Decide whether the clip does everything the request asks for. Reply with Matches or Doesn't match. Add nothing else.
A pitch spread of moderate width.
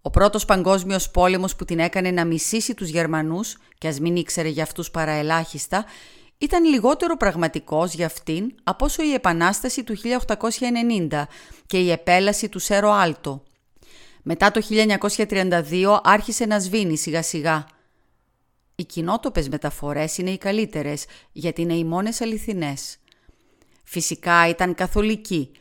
Matches